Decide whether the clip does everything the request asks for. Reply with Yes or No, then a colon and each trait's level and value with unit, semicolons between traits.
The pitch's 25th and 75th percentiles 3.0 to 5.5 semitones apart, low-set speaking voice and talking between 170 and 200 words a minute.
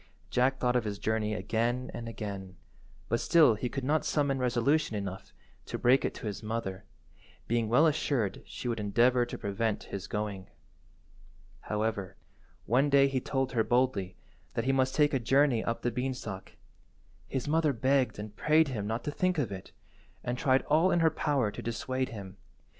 Yes: average, 4.2 semitones; low, 120 Hz; average, 180 wpm